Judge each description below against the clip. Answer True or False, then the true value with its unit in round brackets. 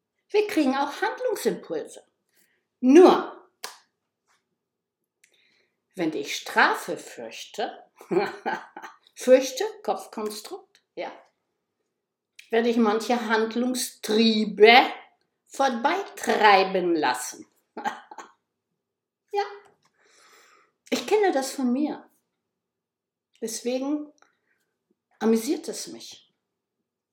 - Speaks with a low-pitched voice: False (275 Hz)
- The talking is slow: True (60 wpm)